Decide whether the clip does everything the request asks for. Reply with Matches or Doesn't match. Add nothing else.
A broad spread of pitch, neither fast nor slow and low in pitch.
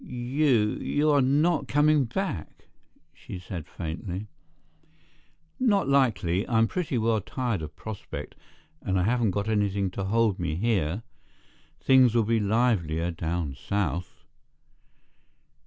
Doesn't match